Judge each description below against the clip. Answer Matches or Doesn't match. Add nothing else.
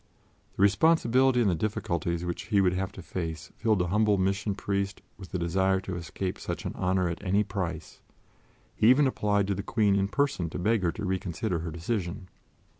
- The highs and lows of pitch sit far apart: Doesn't match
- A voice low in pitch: Matches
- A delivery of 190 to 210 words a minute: Matches